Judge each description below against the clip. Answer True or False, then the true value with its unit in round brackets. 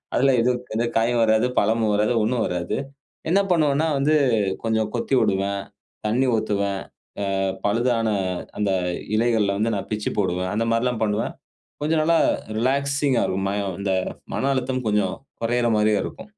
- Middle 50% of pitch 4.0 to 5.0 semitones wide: False (3.4 semitones)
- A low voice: True (115 Hz)